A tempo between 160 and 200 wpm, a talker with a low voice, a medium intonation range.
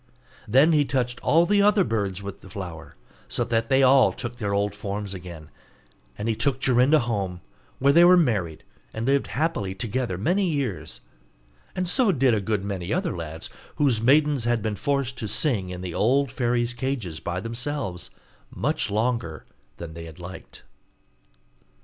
No: average, 170 wpm; low, 115 Hz; wide, 6.1 semitones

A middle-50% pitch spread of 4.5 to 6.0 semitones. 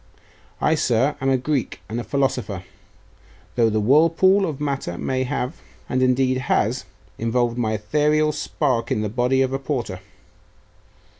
No: average, 3.9 semitones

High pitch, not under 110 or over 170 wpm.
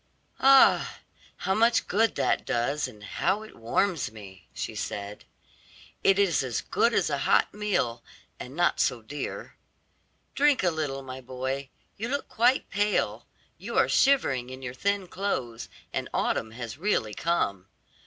No: medium, 140 Hz; average, 155 wpm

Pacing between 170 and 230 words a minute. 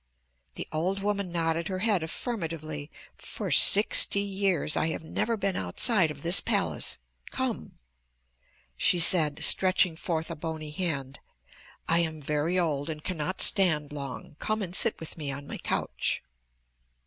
No: average, 150 wpm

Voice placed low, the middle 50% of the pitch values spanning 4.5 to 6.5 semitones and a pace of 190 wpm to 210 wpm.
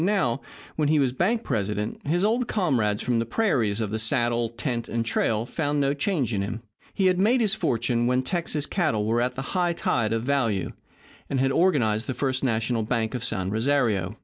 Yes: low, 125 Hz; wide, 5.6 semitones; average, 200 wpm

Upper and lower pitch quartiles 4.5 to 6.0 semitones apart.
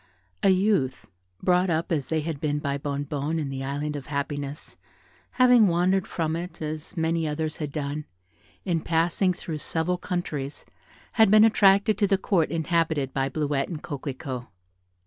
No: average, 3.9 semitones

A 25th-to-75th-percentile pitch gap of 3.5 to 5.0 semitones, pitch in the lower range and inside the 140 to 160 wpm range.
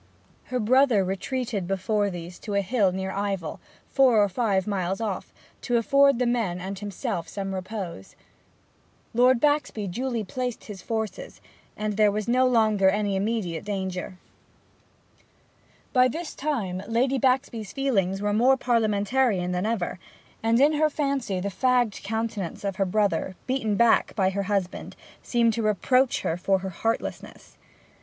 No: average, 4.3 semitones; high, 210 Hz; average, 150 wpm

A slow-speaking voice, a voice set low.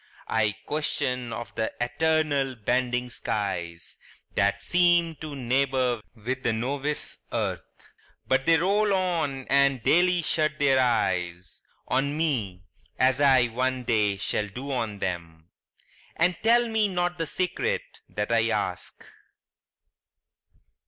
Yes: slow, 125 wpm; low, 130 Hz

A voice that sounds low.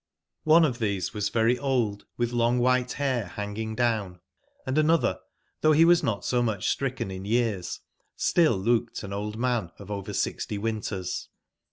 Yes: low, 115 Hz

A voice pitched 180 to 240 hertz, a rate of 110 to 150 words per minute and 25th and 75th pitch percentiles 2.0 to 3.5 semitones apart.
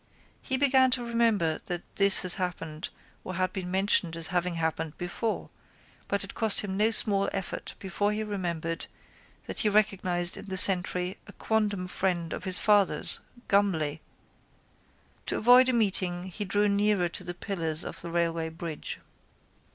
No: high, 190 Hz; average, 160 wpm; average, 3.1 semitones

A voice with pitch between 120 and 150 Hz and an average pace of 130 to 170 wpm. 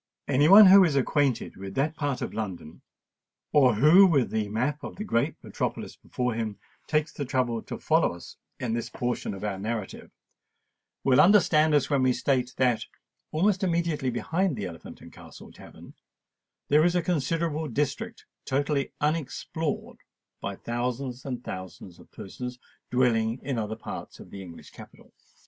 Yes: low, 130 Hz; average, 160 wpm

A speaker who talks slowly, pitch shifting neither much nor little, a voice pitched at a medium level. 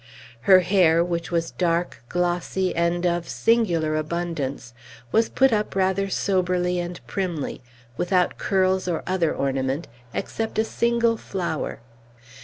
No: slow, 125 wpm; narrow, 2.3 semitones; medium, 175 Hz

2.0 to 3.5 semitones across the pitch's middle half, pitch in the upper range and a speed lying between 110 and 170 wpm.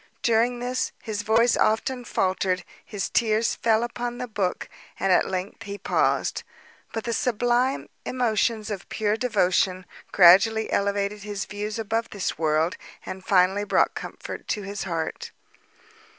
Yes: average, 3.1 semitones; high, 210 Hz; average, 140 wpm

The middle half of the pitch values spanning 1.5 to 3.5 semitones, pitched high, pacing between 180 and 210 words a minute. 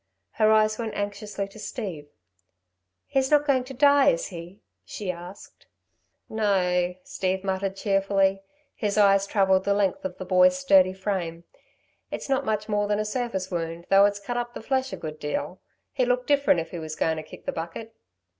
Yes: average, 3.1 semitones; high, 195 Hz; average, 185 wpm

